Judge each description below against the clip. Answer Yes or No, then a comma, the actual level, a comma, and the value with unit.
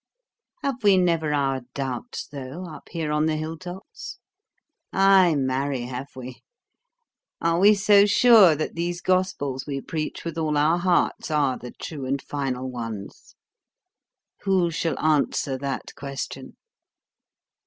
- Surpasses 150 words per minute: No, slow, 135 wpm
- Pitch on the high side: No, medium, 155 Hz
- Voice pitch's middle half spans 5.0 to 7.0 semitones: No, average, 4.6 semitones